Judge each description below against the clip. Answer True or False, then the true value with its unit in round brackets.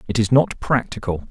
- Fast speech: False (185 wpm)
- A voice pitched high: False (110 Hz)